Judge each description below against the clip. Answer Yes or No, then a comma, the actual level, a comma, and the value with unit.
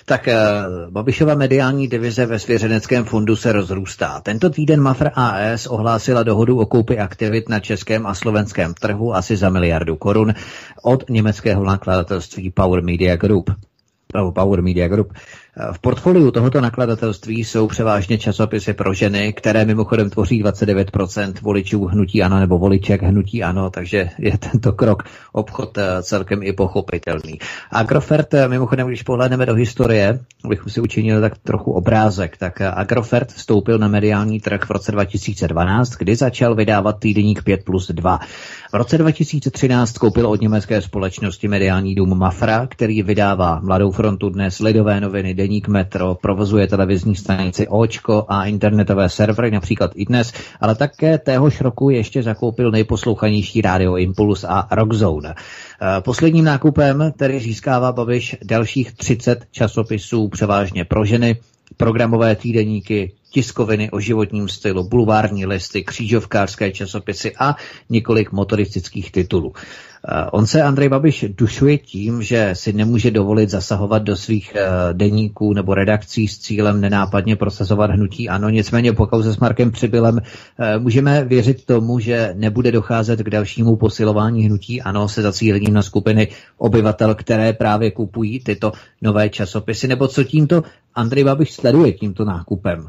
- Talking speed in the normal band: Yes, average, 140 wpm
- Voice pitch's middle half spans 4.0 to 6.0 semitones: No, average, 2.8 semitones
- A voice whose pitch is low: Yes, low, 110 Hz